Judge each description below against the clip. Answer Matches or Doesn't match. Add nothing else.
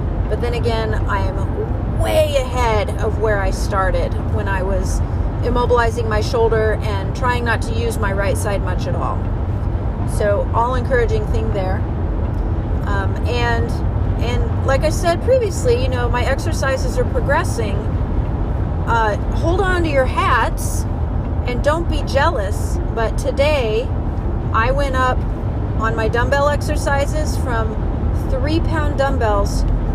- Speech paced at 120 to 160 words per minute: Matches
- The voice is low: Matches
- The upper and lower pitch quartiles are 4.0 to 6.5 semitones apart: Doesn't match